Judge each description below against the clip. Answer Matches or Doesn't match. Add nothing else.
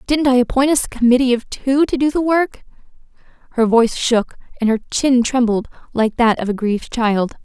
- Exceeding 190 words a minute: Matches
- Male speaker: Doesn't match